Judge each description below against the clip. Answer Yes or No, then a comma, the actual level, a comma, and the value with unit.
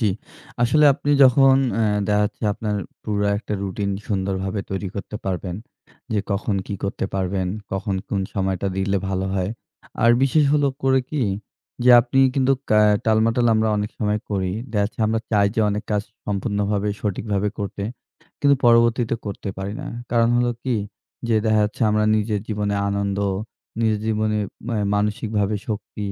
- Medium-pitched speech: No, low, 105 Hz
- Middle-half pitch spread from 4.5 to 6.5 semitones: No, narrow, 2.4 semitones